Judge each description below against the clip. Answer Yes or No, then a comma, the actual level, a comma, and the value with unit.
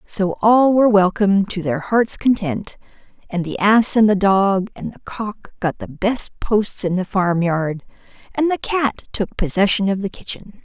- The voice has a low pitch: No, high, 200 Hz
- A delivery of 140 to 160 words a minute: No, average, 180 wpm